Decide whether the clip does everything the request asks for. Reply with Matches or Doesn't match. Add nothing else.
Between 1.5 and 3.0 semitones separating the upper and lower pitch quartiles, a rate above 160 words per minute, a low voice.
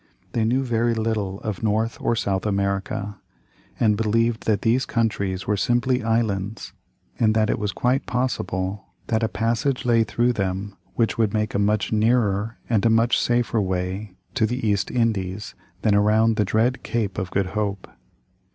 Matches